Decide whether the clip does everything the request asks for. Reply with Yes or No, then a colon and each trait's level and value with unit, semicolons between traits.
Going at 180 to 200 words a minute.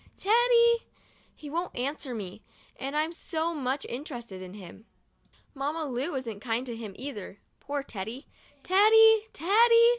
No: average, 150 wpm